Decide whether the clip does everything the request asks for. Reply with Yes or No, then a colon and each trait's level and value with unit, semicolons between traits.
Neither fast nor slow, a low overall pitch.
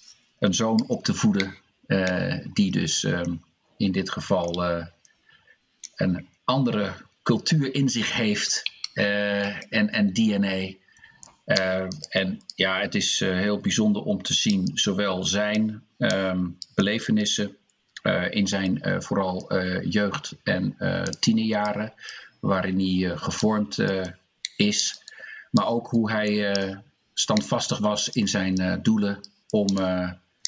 No: slow, 130 wpm; low, 100 Hz